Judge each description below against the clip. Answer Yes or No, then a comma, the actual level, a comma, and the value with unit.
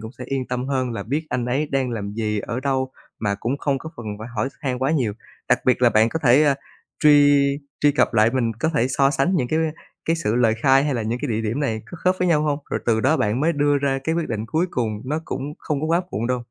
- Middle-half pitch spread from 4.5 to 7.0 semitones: No, average, 4.1 semitones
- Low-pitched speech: Yes, low, 130 Hz